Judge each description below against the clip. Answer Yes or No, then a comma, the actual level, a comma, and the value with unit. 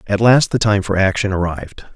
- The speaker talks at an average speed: No, fast, 215 wpm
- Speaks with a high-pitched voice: No, low, 105 Hz